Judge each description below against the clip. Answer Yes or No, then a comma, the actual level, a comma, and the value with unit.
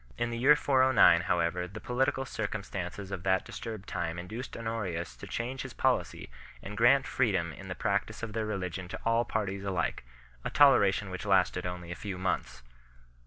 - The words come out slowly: No, average, 175 wpm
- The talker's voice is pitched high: No, low, 100 Hz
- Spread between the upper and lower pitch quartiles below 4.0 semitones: No, average, 4.3 semitones